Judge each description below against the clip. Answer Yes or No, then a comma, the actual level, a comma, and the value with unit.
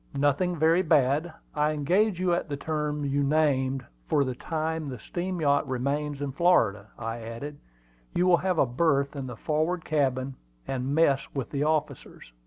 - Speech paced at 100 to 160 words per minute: No, average, 175 wpm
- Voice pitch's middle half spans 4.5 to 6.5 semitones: No, average, 3.1 semitones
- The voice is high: No, medium, 145 Hz